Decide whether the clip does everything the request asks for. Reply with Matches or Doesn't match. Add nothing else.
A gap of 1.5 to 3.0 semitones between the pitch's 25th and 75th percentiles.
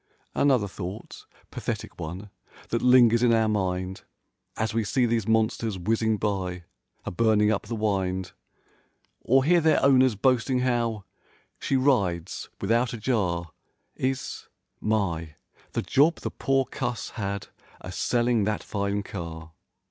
Doesn't match